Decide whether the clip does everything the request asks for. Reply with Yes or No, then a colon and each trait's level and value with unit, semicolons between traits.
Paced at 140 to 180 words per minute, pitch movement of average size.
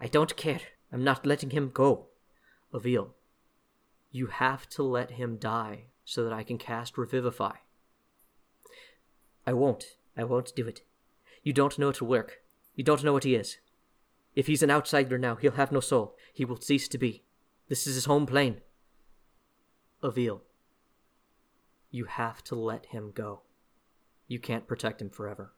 Yes: average, 160 wpm; average, 3.2 semitones